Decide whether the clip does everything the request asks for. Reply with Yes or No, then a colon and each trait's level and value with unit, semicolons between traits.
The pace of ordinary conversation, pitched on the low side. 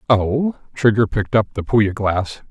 Yes: average, 165 wpm; low, 110 Hz